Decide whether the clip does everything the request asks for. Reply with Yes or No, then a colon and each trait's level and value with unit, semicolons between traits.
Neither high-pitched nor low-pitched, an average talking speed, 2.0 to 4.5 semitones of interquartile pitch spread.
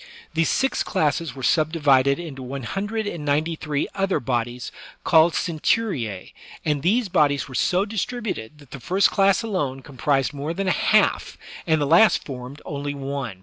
No: medium, 150 Hz; average, 165 wpm; average, 5.2 semitones